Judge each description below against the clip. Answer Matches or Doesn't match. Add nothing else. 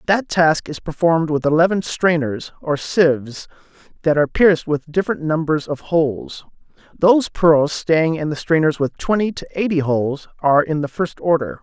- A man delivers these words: Matches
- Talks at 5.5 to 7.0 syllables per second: Doesn't match